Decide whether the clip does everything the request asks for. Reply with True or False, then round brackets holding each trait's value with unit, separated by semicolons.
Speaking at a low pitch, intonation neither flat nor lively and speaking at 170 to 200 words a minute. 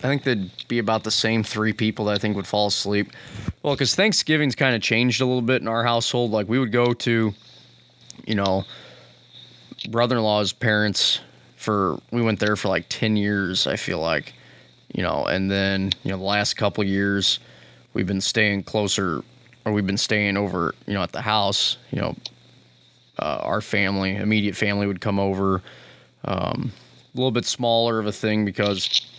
True (105 Hz; 3.0 semitones; 190 wpm)